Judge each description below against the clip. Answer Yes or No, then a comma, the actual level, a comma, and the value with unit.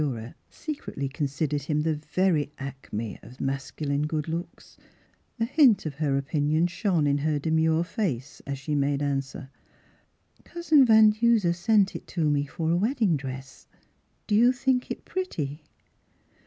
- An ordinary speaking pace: Yes, average, 160 wpm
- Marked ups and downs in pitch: Yes, wide, 5.9 semitones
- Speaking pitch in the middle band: Yes, medium, 155 Hz